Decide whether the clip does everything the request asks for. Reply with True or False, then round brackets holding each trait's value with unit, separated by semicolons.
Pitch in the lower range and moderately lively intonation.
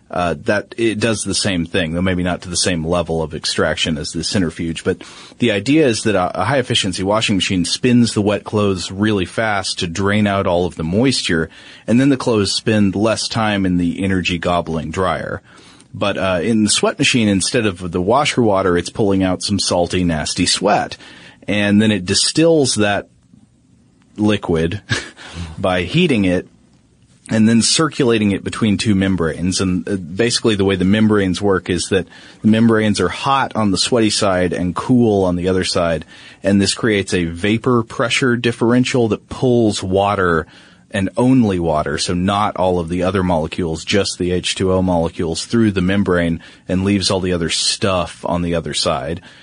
True (95 Hz; 3.6 semitones)